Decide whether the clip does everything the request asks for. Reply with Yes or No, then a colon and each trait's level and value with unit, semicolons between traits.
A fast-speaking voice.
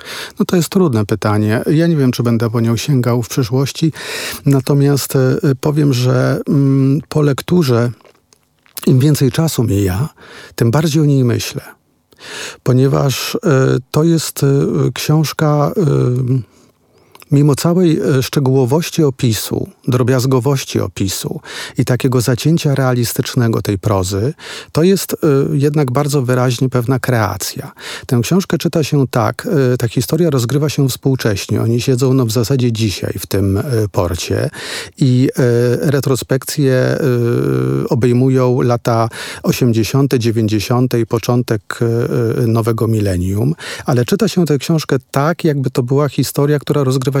No: average, 130 wpm